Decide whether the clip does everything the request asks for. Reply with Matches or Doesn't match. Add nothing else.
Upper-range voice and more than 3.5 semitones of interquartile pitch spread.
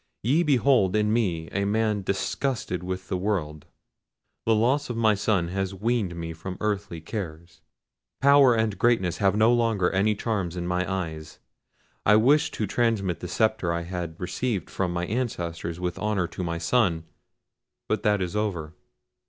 Doesn't match